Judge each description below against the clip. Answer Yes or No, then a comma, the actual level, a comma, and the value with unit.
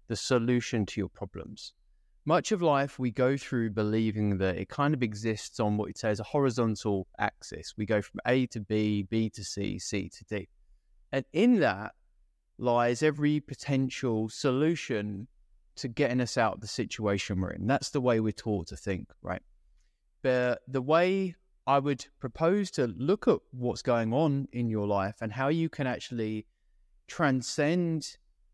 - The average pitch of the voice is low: Yes, low, 115 Hz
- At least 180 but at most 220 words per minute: No, average, 170 wpm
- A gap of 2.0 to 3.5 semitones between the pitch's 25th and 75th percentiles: No, average, 4.9 semitones